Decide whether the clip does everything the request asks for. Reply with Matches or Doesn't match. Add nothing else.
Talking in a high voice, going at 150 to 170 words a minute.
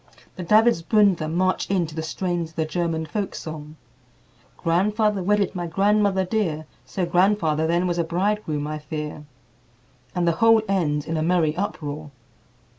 Doesn't match